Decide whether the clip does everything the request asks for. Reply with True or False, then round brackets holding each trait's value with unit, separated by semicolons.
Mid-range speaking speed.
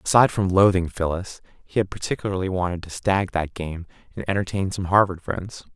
True (175 wpm)